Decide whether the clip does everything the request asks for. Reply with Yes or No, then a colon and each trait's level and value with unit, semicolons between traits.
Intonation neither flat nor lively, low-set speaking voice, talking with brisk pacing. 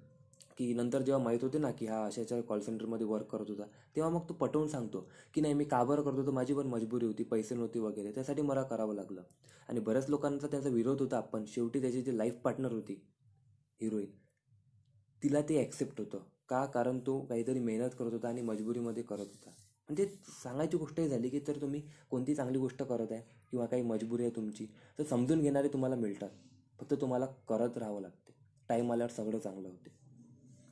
Yes: average, 3.3 semitones; low, 120 Hz; fast, 190 wpm